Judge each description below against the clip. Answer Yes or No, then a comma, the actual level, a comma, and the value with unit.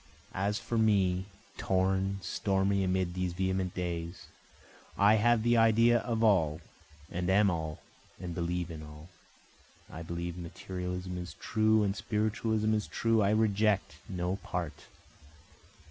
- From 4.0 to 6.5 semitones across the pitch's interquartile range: No, average, 3.3 semitones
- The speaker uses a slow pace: Yes, slow, 130 wpm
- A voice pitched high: No, very low, 95 Hz